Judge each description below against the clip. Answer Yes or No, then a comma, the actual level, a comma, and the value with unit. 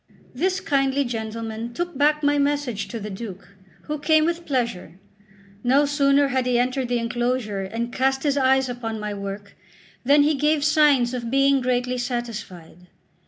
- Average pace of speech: Yes, average, 165 wpm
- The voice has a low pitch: No, very high, 255 Hz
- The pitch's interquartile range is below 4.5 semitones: Yes, average, 3.7 semitones